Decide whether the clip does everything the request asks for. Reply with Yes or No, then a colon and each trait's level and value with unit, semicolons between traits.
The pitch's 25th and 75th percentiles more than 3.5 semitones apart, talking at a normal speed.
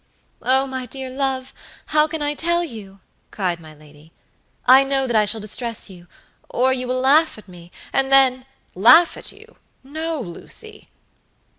Yes: average, 4.7 semitones; average, 160 wpm